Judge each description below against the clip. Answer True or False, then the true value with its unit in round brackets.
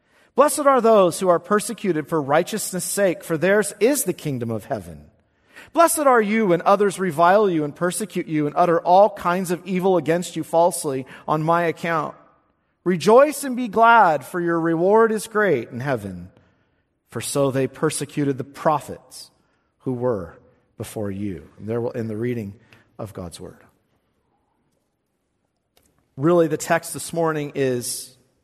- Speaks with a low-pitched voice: False (165 Hz)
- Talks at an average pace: True (155 wpm)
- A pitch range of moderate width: False (7.0 semitones)